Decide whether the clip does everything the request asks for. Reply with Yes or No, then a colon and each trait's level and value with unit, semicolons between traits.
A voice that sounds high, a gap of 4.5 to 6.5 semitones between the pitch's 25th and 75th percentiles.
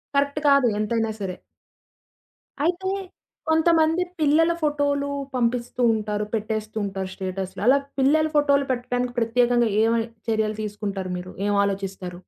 Yes: high, 230 Hz; wide, 5.6 semitones